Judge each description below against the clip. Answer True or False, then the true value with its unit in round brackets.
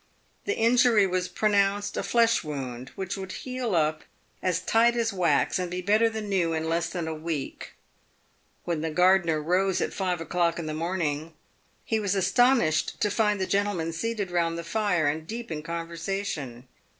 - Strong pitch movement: False (4.1 semitones)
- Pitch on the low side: False (180 Hz)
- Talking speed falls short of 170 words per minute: False (175 wpm)